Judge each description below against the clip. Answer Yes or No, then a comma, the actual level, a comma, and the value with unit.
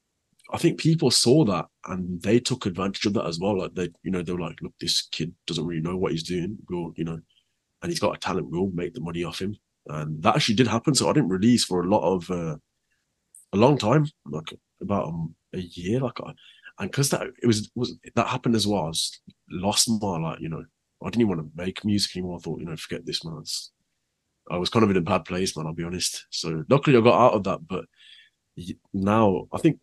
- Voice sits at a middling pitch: No, very low, 95 Hz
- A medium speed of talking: No, fast, 250 wpm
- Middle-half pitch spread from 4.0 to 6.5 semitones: Yes, average, 5.1 semitones